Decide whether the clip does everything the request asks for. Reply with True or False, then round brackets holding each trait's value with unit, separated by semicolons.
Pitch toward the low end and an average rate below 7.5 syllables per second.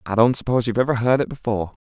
False (120 Hz; 8.3 syllables/s)